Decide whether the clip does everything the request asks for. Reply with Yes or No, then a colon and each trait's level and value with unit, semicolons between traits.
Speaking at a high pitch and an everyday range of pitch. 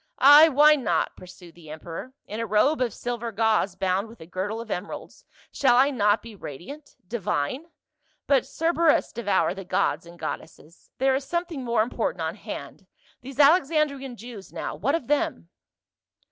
No: high, 235 Hz; wide, 6.7 semitones